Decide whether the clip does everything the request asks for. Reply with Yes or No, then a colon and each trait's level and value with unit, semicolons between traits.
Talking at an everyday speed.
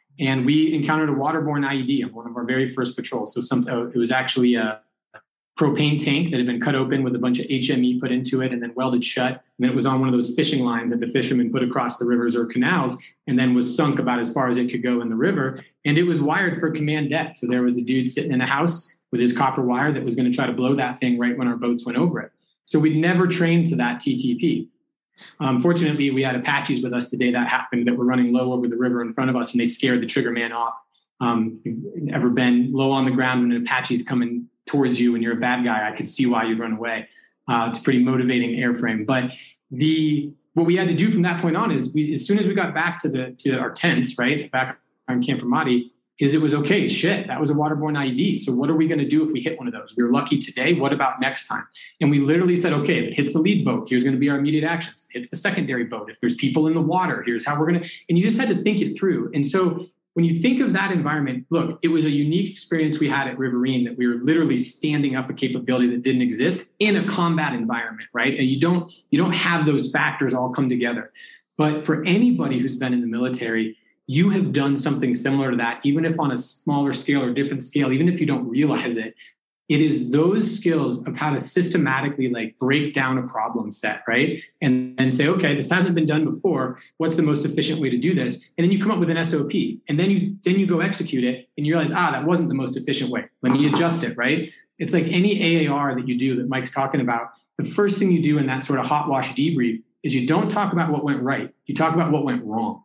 No: fast, 265 wpm